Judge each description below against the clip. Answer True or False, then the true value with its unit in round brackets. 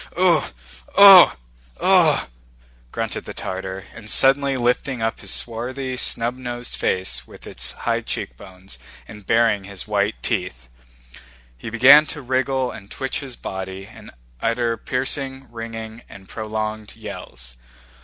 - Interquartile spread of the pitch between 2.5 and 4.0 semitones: False (4.9 semitones)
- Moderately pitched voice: False (115 Hz)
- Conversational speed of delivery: False (130 wpm)